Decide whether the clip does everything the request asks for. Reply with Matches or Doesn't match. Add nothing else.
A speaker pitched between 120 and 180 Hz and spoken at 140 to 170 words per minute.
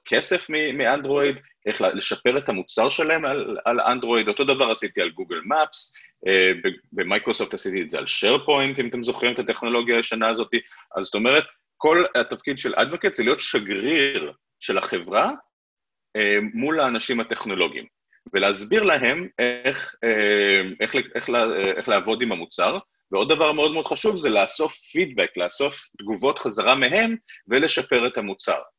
Matches